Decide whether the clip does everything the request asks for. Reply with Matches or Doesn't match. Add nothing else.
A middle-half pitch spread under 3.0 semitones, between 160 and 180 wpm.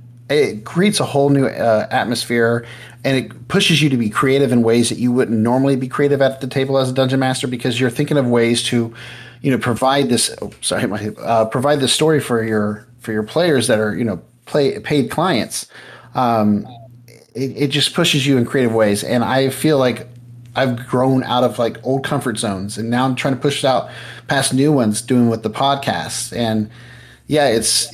Doesn't match